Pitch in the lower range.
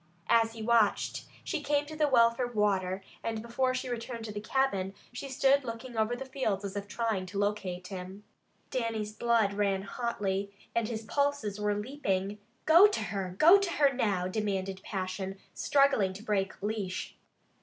No: high, 215 Hz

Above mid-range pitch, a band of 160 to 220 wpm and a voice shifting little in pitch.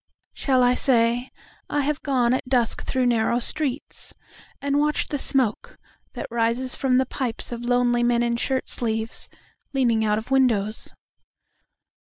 No: high, 245 Hz; average, 140 wpm; narrow, 2.2 semitones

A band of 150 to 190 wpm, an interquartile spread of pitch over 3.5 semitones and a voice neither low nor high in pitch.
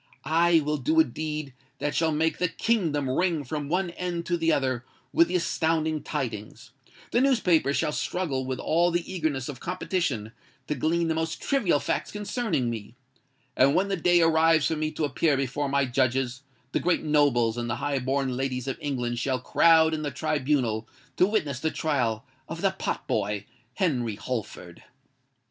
Yes: average, 175 wpm; average, 4.3 semitones; medium, 150 Hz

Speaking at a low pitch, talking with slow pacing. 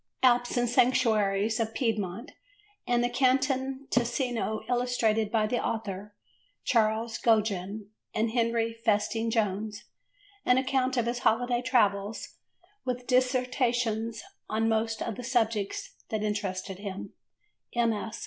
No: high, 230 Hz; slow, 120 wpm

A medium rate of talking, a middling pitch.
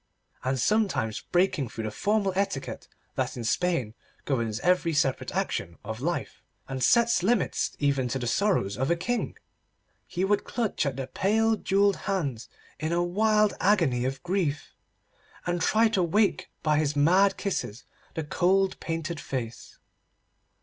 Yes: average, 150 wpm; medium, 170 Hz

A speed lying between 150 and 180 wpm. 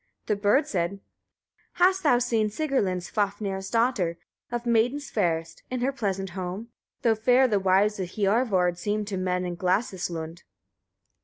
Yes: average, 155 wpm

